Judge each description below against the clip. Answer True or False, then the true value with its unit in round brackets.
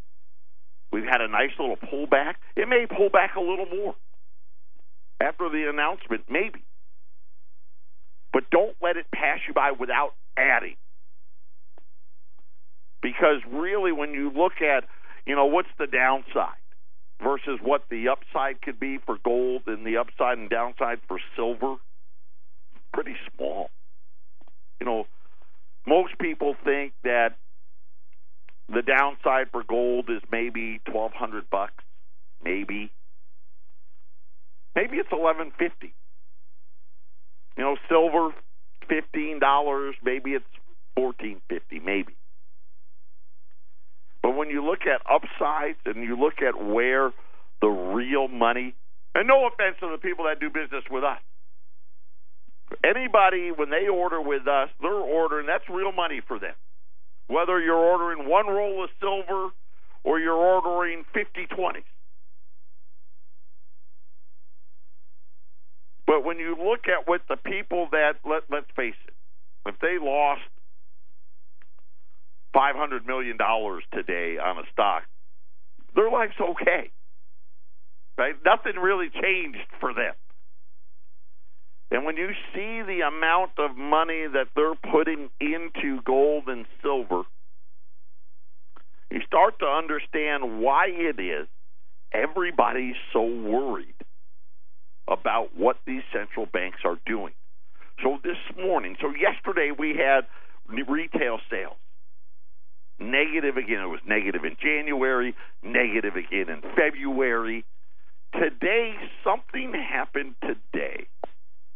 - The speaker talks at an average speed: False (120 wpm)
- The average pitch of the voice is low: True (125 Hz)